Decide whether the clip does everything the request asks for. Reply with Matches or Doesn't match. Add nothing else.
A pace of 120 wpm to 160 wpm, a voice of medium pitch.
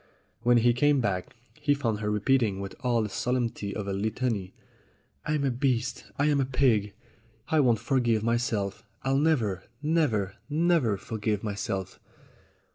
Doesn't match